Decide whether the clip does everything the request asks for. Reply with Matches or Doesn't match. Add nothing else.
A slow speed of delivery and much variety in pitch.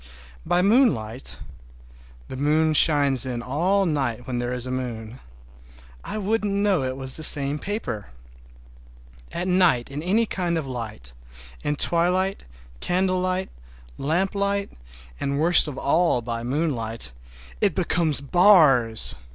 Matches